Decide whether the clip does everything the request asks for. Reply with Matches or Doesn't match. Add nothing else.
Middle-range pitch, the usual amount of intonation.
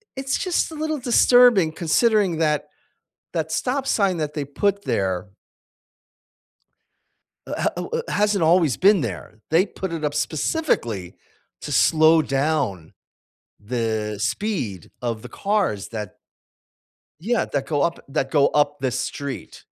Doesn't match